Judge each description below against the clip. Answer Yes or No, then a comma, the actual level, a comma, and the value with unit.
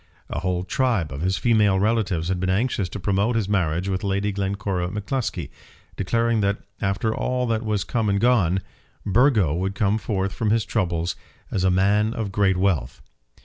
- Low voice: Yes, low, 100 Hz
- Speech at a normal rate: Yes, average, 180 wpm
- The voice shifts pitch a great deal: No, average, 3.0 semitones